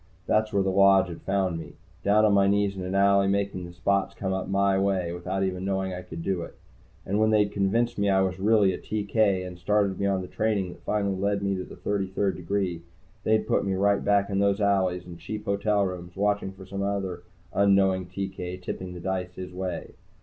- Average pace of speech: No, fast, 225 wpm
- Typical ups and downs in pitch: No, narrow, 1.4 semitones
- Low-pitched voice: Yes, very low, 95 Hz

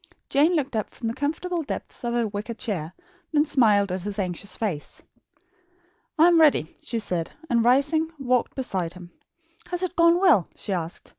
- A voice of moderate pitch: No, high, 235 Hz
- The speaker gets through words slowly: No, average, 175 wpm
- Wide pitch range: Yes, wide, 7.6 semitones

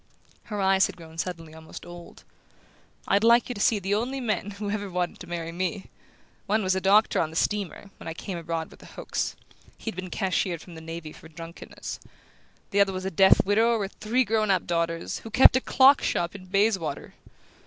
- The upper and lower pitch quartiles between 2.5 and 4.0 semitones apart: Yes, average, 3.7 semitones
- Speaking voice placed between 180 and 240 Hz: Yes, high, 190 Hz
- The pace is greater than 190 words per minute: Yes, fast, 205 wpm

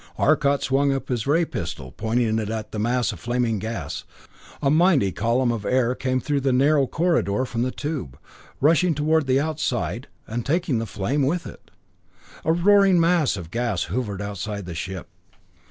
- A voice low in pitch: Yes, low, 125 Hz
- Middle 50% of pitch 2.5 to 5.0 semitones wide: No, wide, 5.6 semitones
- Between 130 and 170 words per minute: No, average, 180 wpm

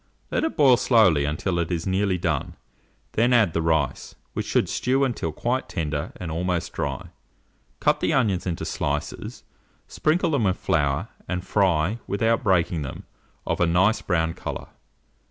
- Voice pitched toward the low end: Yes, very low, 90 Hz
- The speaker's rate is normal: Yes, average, 160 wpm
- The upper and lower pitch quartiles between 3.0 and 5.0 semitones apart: No, wide, 5.5 semitones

